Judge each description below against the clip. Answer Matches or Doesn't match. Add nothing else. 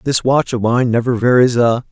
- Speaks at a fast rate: Matches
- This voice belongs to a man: Matches